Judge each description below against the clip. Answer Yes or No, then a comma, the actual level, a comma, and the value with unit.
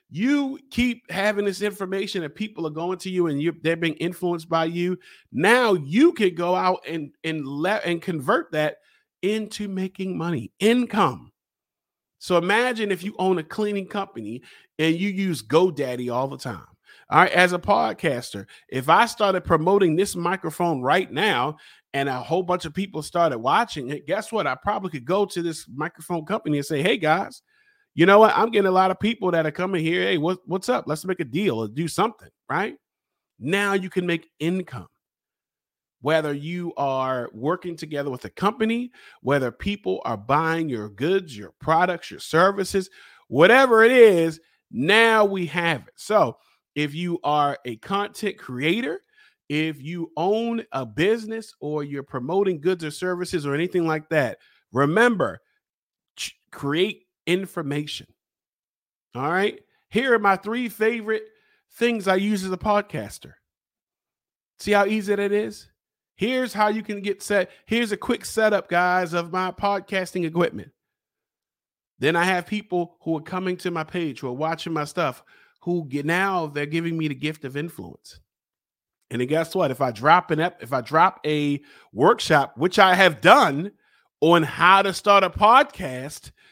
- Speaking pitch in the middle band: Yes, medium, 180 Hz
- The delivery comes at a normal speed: Yes, average, 170 wpm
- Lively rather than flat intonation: No, average, 4.4 semitones